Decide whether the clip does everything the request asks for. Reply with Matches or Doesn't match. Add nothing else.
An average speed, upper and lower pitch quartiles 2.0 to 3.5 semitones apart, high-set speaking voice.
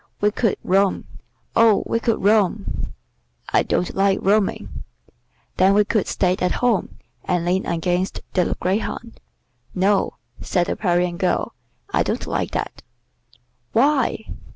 Doesn't match